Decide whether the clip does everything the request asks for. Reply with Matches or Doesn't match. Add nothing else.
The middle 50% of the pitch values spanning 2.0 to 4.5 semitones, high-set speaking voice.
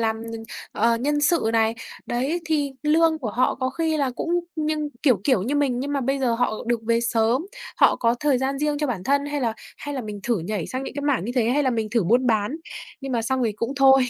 Matches